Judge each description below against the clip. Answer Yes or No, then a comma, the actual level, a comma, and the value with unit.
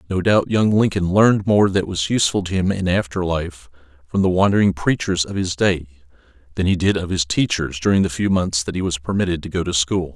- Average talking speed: No, fast, 230 wpm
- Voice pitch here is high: No, very low, 90 Hz